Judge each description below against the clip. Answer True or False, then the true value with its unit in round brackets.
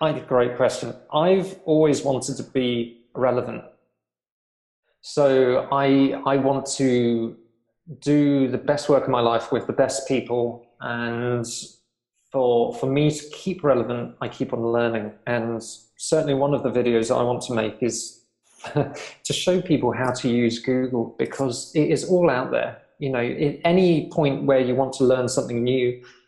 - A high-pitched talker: False (130 Hz)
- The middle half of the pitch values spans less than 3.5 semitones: True (3.0 semitones)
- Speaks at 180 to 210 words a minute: False (170 wpm)